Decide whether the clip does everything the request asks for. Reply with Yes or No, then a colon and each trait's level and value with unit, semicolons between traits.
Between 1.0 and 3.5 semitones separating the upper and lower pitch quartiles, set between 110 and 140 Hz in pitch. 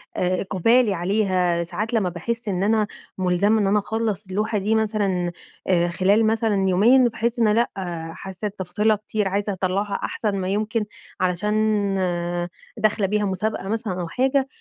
No: average, 2.8 semitones; high, 205 Hz